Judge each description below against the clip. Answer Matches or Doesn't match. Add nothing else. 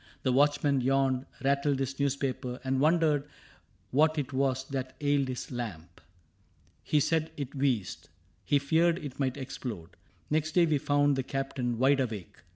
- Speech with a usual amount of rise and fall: Doesn't match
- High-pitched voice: Doesn't match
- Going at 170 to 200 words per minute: Doesn't match